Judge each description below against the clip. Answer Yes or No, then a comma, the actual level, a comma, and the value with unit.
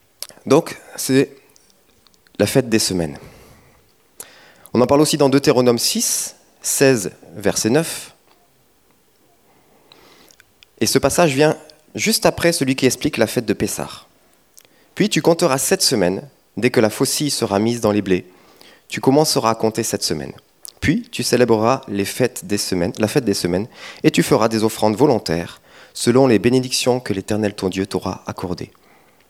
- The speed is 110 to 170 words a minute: Yes, average, 155 wpm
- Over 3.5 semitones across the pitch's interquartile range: Yes, average, 5.2 semitones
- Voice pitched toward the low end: Yes, low, 120 Hz